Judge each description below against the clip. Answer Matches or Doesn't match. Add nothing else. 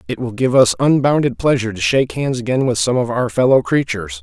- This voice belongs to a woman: Doesn't match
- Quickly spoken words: Matches